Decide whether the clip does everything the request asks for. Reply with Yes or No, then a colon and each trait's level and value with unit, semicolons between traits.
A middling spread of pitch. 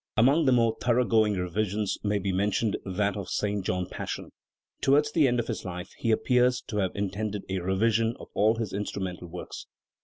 Yes: average, 3.3 semitones